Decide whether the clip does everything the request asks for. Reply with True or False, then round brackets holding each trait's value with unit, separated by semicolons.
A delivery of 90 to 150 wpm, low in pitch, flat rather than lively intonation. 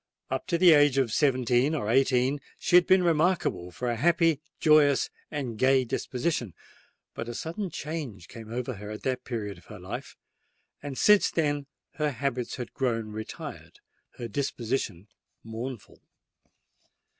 False (145 wpm; 130 Hz; 4.6 semitones)